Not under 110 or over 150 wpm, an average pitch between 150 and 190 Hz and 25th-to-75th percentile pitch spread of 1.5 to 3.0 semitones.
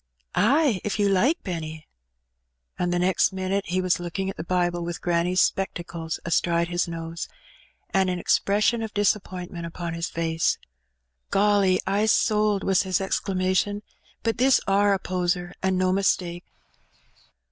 Yes: average, 145 wpm; medium, 185 Hz; narrow, 2.5 semitones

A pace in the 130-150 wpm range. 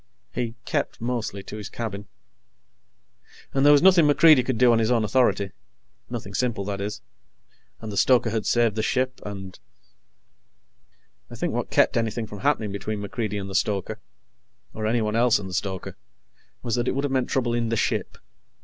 No: average, 185 wpm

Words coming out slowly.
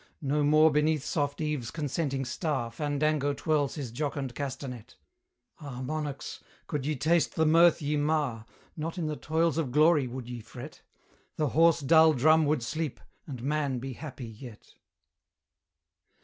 No: average, 150 wpm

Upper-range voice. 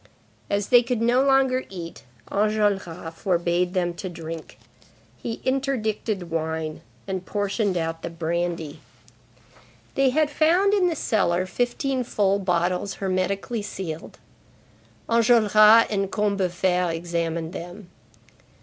Yes: high, 195 Hz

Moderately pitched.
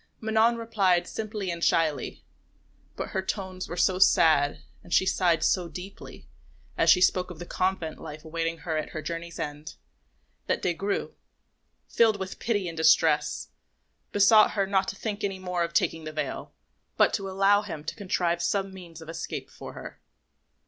Yes: medium, 180 Hz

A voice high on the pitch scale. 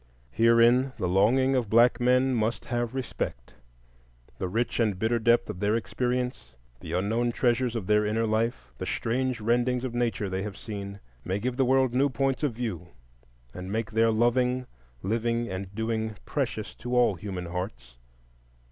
No: low, 115 Hz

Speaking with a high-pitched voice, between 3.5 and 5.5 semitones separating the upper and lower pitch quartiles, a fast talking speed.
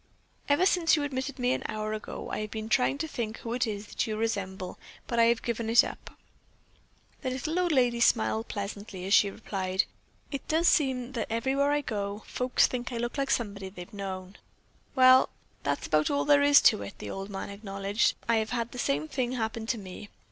Yes: high, 230 Hz; average, 4.4 semitones; fast, 210 wpm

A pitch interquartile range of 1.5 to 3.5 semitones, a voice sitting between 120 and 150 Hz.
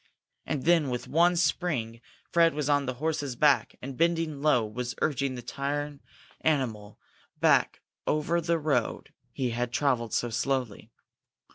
No: average, 4.1 semitones; medium, 140 Hz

